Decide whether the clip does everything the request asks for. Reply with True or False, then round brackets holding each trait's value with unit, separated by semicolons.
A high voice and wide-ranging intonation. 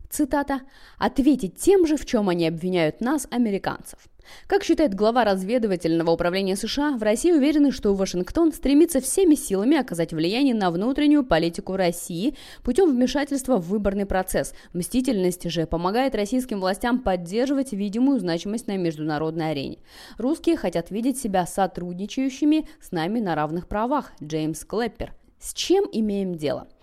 True (215 Hz; 7.3 semitones)